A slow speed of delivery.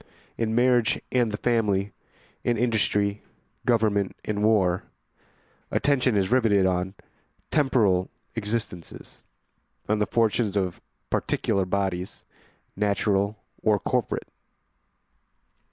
Yes: slow, 95 wpm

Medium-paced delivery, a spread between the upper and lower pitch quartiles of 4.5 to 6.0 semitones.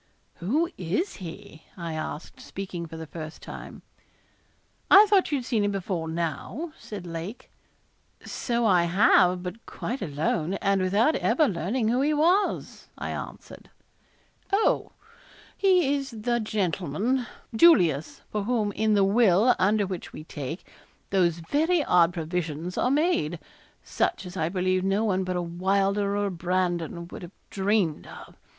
Yes: average, 150 wpm; wide, 5.4 semitones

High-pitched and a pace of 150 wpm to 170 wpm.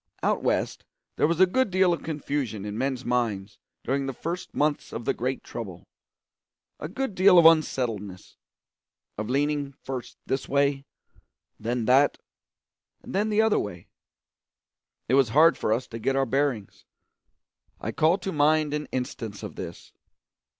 No: low, 135 Hz; average, 155 wpm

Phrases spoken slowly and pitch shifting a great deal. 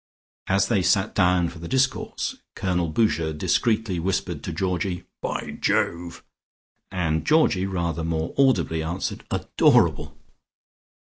No: slow, 120 wpm; average, 2.8 semitones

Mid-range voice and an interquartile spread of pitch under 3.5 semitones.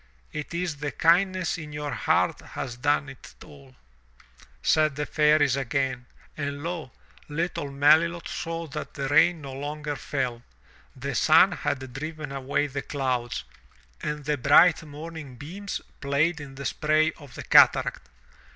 Yes: medium, 145 Hz; narrow, 2.5 semitones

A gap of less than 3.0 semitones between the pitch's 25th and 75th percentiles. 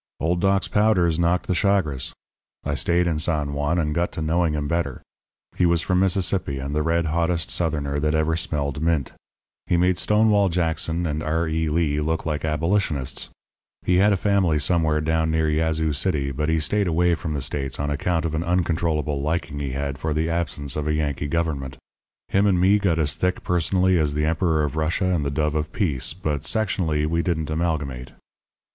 Yes: narrow, 2.6 semitones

